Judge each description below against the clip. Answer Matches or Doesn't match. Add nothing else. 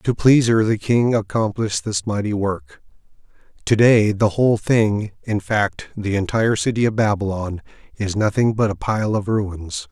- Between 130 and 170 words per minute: Matches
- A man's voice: Matches